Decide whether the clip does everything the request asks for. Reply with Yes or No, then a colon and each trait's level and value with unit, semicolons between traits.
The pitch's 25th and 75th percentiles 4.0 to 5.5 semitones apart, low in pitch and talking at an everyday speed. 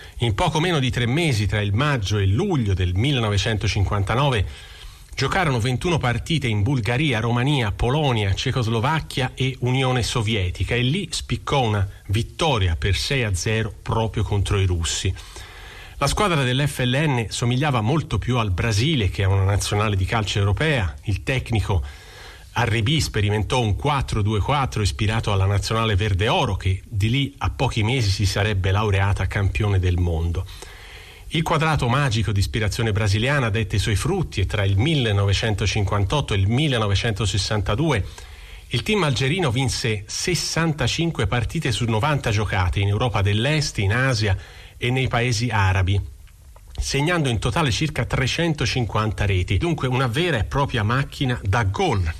Yes: average, 4.8 semitones; low, 110 Hz; average, 145 wpm